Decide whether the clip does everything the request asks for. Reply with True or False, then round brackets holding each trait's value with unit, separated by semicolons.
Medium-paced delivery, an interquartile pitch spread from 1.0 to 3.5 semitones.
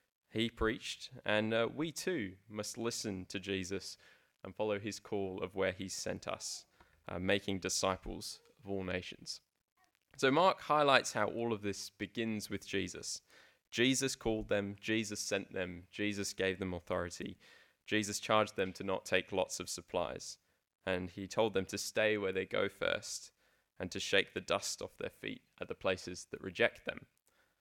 True (170 wpm; 2.5 semitones)